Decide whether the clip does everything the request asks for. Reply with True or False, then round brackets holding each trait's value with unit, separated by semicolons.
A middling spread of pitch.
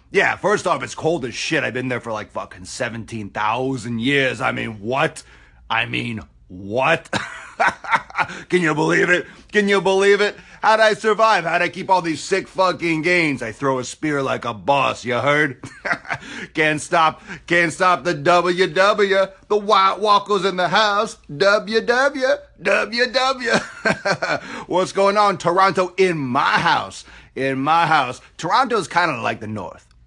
False (7.2 semitones)